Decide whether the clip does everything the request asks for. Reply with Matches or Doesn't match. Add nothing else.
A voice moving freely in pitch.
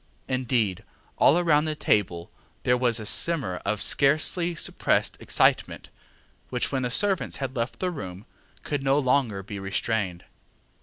Matches